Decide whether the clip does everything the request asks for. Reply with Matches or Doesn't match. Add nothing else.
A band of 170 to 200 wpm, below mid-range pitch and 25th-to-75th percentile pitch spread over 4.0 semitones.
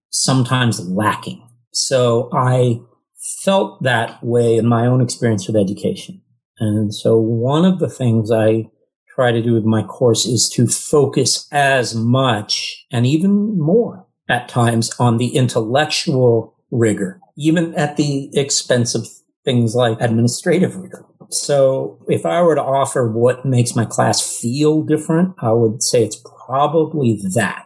Doesn't match